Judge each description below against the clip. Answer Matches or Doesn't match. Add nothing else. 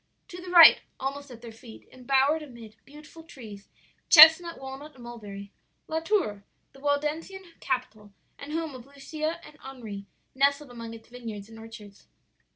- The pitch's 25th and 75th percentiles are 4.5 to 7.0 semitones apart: Matches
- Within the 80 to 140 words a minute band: Doesn't match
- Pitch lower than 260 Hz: Doesn't match